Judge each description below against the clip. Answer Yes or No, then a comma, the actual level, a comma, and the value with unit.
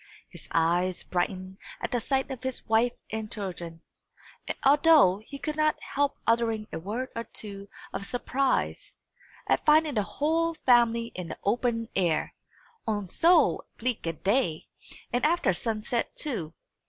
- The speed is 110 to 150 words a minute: Yes, average, 145 wpm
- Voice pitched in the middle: No, high, 230 Hz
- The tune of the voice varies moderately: No, wide, 5.7 semitones